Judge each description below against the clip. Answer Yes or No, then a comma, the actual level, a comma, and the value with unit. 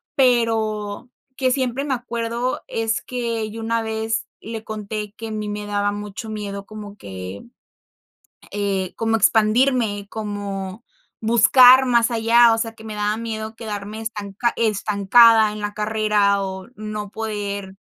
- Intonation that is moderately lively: No, narrow, 1.9 semitones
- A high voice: Yes, high, 220 Hz